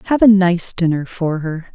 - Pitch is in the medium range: Yes, medium, 180 Hz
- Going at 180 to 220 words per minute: Yes, fast, 205 wpm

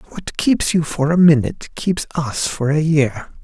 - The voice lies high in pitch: No, medium, 150 Hz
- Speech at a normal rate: Yes, average, 190 wpm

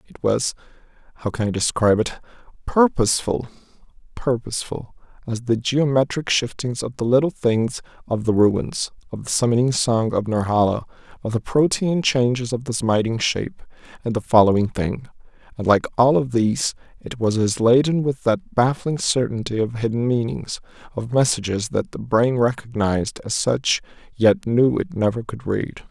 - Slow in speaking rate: No, average, 155 wpm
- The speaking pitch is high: No, low, 120 Hz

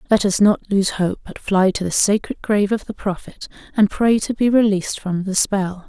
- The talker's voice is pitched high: Yes, high, 200 Hz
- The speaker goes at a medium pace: No, fast, 225 wpm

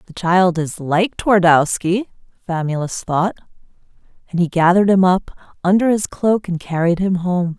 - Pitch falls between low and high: Yes, medium, 180 Hz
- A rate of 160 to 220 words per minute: No, average, 150 wpm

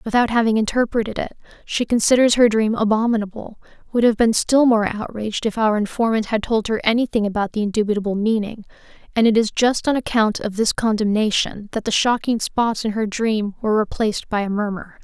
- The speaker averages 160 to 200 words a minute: Yes, average, 190 wpm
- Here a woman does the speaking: Yes, female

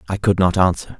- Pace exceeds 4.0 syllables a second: Yes, 6.2 syllables/s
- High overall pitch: No, very low, 95 Hz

